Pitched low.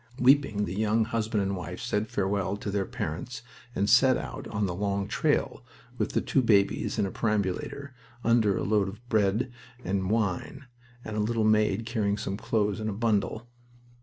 Yes: low, 105 Hz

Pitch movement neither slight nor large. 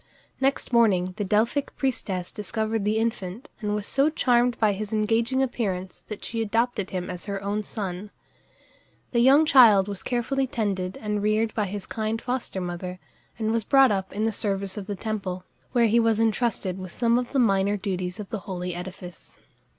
Yes: average, 3.4 semitones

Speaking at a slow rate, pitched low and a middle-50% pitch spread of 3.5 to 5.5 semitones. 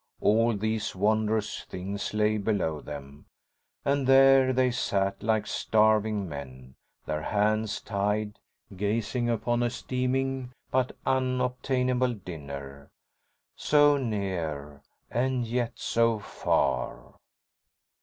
Yes: slow, 100 wpm; low, 110 Hz; average, 4.5 semitones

